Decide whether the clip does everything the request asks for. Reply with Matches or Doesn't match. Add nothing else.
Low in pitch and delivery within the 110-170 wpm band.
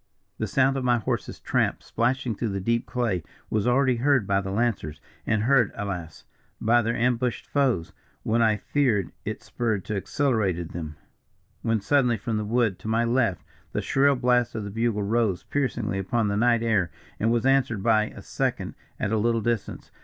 Doesn't match